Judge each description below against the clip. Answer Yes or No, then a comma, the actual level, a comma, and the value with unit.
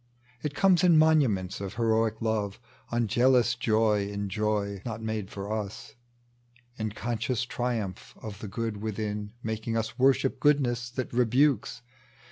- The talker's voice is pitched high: No, low, 110 Hz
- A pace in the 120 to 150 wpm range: Yes, average, 140 wpm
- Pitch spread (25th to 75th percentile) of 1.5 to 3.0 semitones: Yes, narrow, 2.6 semitones